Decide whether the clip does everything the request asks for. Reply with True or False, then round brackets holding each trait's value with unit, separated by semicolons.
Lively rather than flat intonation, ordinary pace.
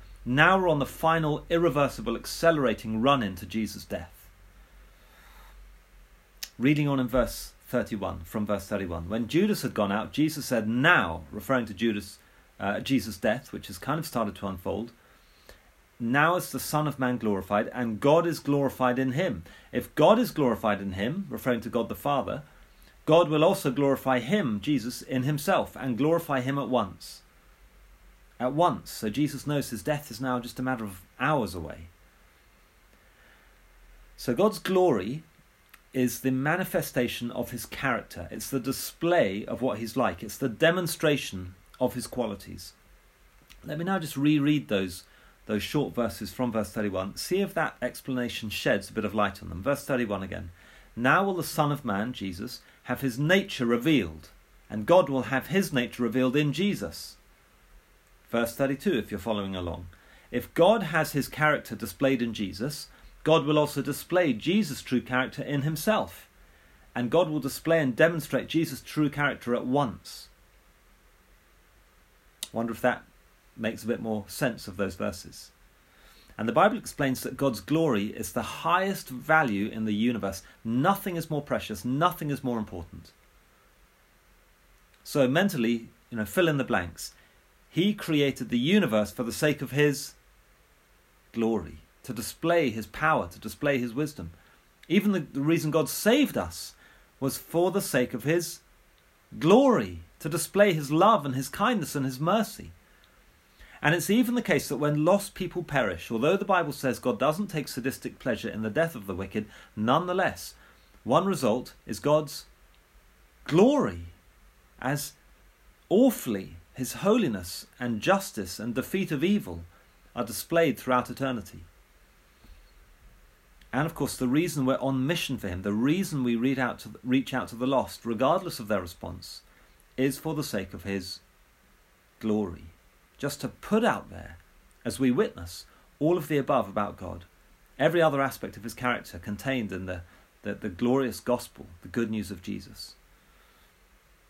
True (7.5 semitones; 160 wpm)